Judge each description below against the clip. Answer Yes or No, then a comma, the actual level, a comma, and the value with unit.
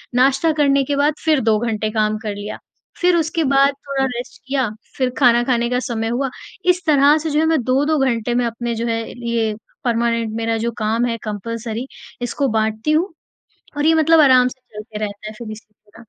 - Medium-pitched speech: No, high, 245 Hz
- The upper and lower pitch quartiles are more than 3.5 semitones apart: Yes, average, 3.9 semitones